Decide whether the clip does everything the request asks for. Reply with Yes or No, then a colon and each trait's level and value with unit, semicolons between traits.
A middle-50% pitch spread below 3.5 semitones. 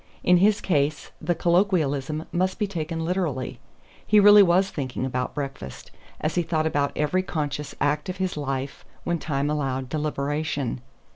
No: average, 4.2 semitones